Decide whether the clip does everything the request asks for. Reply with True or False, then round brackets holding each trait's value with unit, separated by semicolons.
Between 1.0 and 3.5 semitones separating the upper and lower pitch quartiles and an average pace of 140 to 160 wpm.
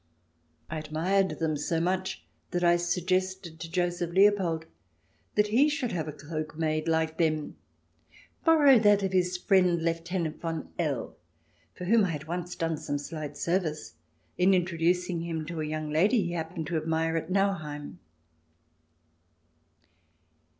True (2.7 semitones; 150 wpm)